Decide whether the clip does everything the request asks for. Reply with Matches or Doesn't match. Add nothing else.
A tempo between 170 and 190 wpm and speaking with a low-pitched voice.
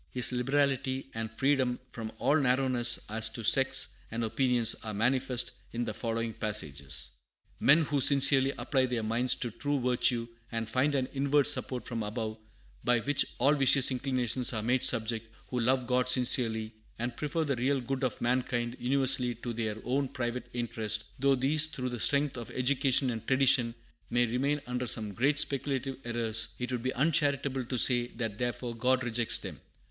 Matches